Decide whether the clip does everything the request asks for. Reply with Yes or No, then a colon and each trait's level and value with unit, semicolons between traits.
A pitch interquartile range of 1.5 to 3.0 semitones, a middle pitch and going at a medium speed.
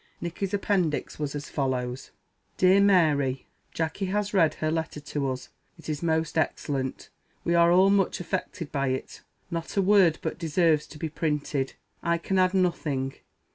No: average, 4.0 semitones; medium, 160 Hz; average, 165 wpm